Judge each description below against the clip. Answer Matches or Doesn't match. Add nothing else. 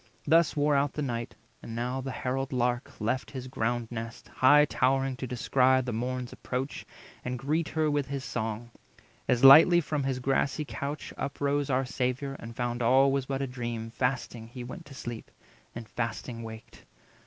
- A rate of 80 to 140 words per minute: Doesn't match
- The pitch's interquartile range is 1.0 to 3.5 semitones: Matches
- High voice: Doesn't match